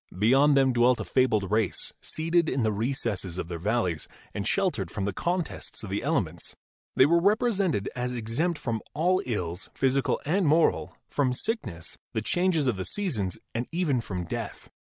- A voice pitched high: No, low, 125 Hz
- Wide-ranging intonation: Yes, wide, 8.1 semitones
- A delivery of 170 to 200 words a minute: Yes, average, 175 wpm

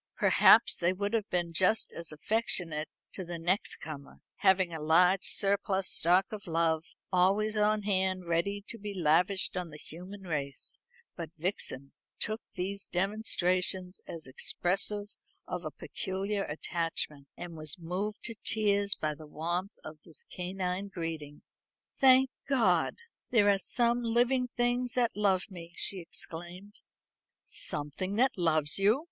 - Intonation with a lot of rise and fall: No, average, 3.5 semitones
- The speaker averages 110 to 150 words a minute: Yes, average, 140 wpm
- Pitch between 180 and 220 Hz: Yes, medium, 185 Hz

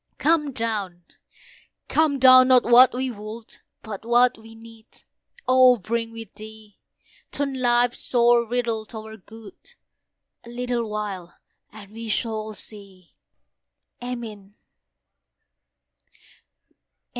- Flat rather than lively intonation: Yes, narrow, 2.3 semitones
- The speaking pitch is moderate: No, high, 230 Hz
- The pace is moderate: No, slow, 110 wpm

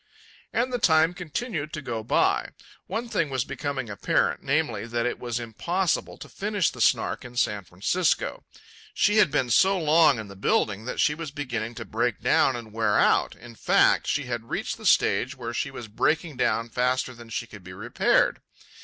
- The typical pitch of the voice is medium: No, low, 125 Hz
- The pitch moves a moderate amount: No, wide, 5.8 semitones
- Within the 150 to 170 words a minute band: No, average, 190 wpm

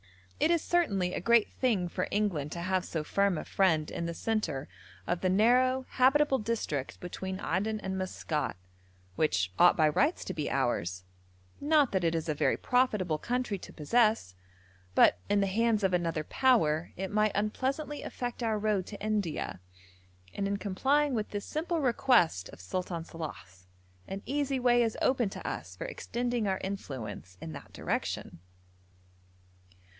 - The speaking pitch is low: No, high, 200 Hz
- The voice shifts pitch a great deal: Yes, wide, 6.6 semitones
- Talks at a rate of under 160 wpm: No, average, 165 wpm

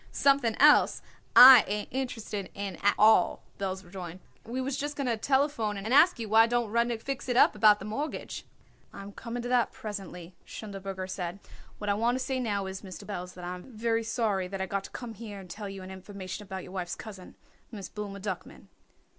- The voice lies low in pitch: No, high, 210 Hz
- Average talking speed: No, fast, 210 wpm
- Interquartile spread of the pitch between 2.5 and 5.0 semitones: Yes, average, 3.7 semitones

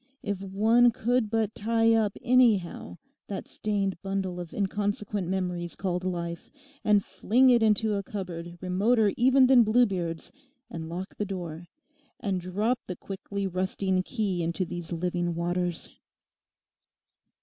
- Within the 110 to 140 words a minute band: Yes, slow, 135 wpm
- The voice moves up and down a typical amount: Yes, average, 3.4 semitones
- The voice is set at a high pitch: Yes, high, 195 Hz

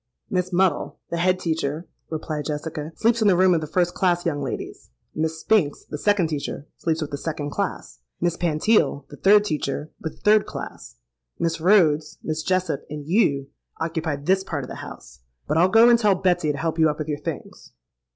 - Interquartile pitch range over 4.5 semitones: No, average, 3.5 semitones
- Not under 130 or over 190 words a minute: No, average, 200 wpm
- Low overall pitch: No, medium, 165 Hz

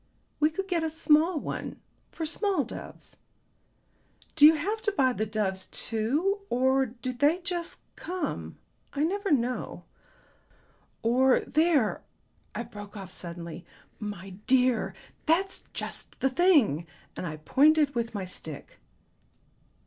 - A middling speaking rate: No, slow, 130 wpm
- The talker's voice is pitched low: No, very high, 265 Hz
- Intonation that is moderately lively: No, wide, 7.2 semitones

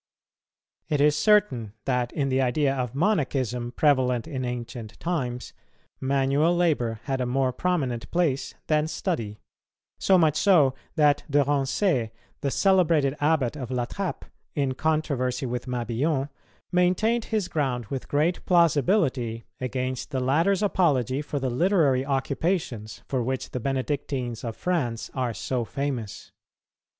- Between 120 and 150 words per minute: Yes, slow, 135 wpm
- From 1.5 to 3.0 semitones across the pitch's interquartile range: No, average, 4.1 semitones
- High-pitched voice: No, low, 135 Hz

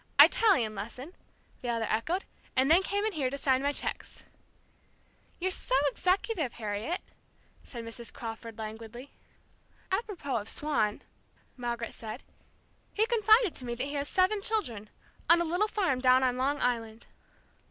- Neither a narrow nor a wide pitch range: No, wide, 7.9 semitones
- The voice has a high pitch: Yes, very high, 265 Hz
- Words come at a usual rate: Yes, average, 150 wpm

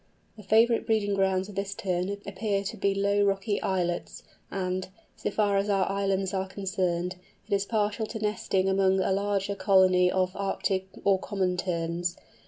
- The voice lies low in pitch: No, high, 195 Hz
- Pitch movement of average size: No, narrow, 1.4 semitones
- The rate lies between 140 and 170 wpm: Yes, average, 160 wpm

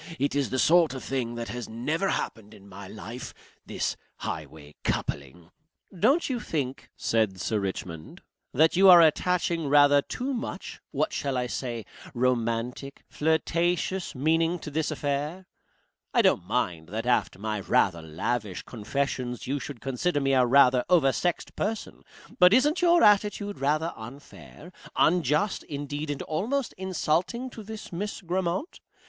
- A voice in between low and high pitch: Yes, medium, 145 Hz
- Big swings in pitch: Yes, wide, 6.8 semitones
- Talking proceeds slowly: No, average, 150 wpm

